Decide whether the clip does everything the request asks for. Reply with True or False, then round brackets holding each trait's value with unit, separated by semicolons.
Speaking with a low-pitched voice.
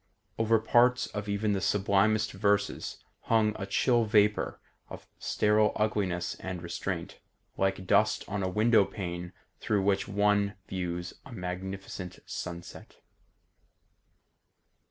True (100 Hz)